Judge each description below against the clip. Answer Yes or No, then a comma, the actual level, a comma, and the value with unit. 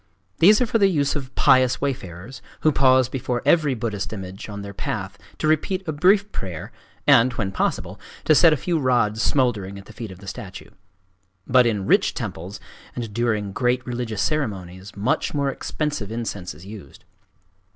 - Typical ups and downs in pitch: No, wide, 5.9 semitones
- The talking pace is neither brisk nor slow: Yes, average, 175 wpm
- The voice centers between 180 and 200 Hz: No, low, 120 Hz